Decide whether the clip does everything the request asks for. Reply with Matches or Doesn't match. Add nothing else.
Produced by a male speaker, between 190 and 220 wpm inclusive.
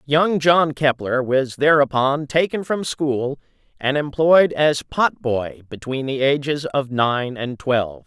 Doesn't match